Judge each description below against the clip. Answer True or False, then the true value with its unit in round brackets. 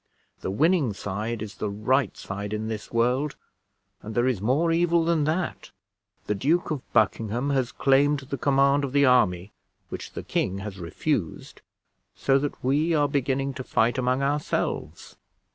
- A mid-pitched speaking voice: False (130 Hz)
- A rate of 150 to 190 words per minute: True (160 wpm)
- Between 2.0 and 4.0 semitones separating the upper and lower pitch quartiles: False (5.0 semitones)